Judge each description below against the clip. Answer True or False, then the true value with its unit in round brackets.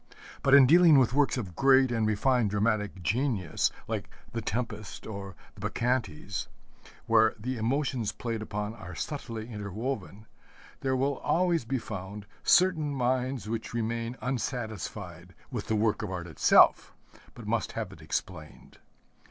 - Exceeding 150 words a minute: False (145 wpm)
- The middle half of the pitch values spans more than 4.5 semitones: False (4.1 semitones)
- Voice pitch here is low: True (115 Hz)